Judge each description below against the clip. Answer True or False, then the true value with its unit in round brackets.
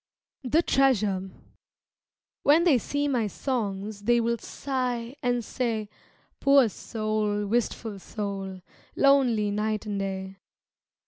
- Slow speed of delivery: True (110 wpm)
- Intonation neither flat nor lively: True (3.8 semitones)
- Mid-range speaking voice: False (225 Hz)